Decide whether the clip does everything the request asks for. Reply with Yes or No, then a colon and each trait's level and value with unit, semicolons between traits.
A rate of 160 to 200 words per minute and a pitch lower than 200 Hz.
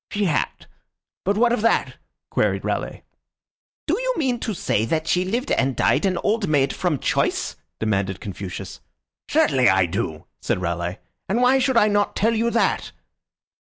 Yes: average, 165 wpm; medium, 185 Hz